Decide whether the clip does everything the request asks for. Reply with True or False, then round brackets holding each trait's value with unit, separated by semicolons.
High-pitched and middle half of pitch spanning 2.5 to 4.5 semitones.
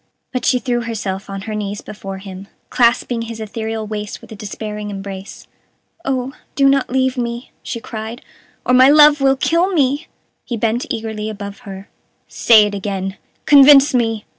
True (225 Hz; 3.8 semitones)